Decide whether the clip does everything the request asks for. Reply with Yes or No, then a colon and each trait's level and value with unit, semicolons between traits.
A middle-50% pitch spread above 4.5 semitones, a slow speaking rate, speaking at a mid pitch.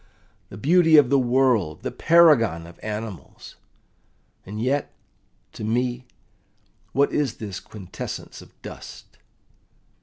No: average, 5.0 semitones; slow, 115 wpm; low, 120 Hz